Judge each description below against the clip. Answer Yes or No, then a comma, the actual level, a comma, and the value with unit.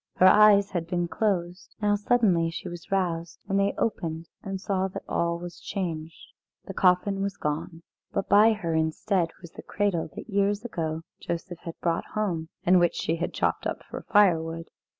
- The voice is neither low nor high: Yes, medium, 180 Hz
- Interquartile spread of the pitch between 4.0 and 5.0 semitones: No, average, 3.2 semitones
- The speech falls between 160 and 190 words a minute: Yes, average, 180 wpm